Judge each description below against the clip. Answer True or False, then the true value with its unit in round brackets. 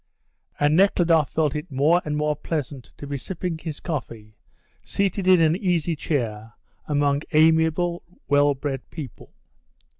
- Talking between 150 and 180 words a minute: False (140 wpm)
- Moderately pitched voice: True (150 Hz)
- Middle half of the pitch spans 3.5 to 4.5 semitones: False (2.8 semitones)